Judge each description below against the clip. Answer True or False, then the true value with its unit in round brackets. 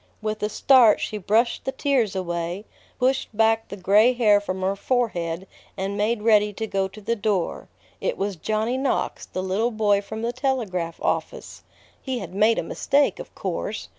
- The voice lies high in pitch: True (215 Hz)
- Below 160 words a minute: False (180 wpm)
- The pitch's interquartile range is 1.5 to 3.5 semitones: True (3.2 semitones)